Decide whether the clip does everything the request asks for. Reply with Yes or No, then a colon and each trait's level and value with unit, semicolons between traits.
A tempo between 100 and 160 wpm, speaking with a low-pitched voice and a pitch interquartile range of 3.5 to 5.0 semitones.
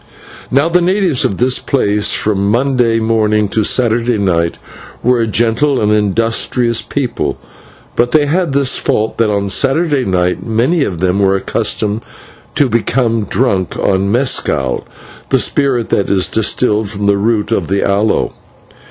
Yes: average, 155 wpm; low, 115 Hz; average, 4.0 semitones